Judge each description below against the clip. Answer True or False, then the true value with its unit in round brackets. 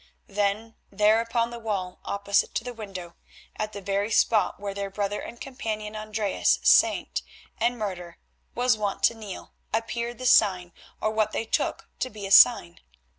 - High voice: True (215 Hz)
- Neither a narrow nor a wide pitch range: False (2.3 semitones)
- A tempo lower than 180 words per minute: True (170 wpm)